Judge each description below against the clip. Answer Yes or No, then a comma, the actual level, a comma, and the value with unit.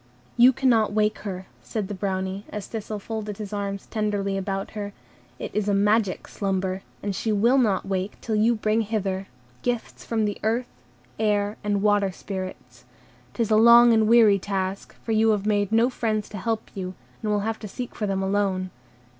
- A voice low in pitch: No, high, 210 Hz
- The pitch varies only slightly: Yes, narrow, 2.0 semitones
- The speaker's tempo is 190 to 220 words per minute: Yes, average, 195 wpm